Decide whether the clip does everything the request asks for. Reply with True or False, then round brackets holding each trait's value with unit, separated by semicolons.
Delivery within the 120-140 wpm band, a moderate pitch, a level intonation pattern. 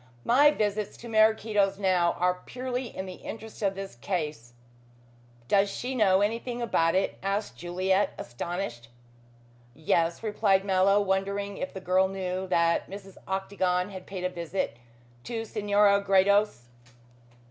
False (135 wpm; 195 Hz; 2.3 semitones)